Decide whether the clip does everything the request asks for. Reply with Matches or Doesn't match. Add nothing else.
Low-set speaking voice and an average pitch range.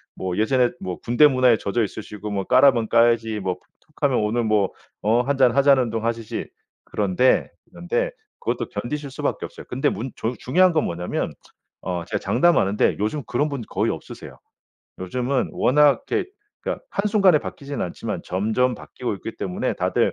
Matches